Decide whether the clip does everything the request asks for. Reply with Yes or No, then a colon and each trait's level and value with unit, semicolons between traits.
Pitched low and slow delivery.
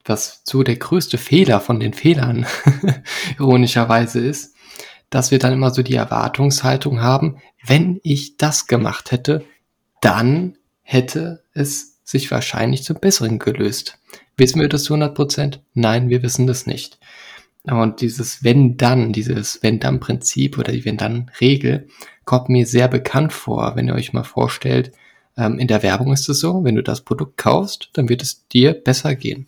No: low, 130 Hz; average, 165 wpm